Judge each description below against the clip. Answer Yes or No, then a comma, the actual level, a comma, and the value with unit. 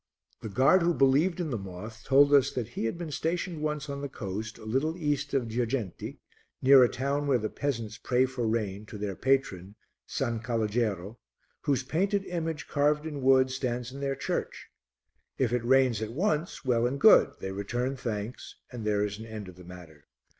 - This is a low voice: Yes, low, 125 Hz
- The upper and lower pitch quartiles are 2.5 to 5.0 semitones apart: Yes, average, 4.7 semitones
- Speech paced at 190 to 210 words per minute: Yes, average, 195 wpm